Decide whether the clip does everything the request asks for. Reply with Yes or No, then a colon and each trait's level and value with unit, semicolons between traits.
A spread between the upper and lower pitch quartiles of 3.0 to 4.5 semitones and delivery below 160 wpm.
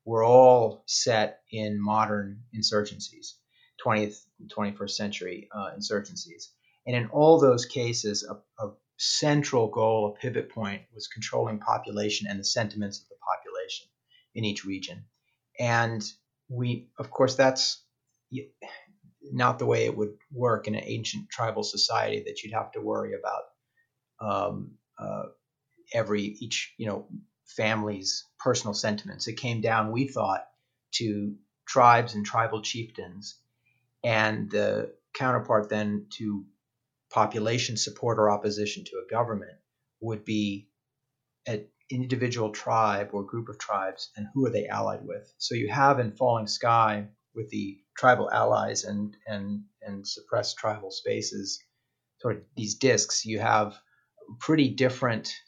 Yes: average, 3.5 semitones; slow, 135 wpm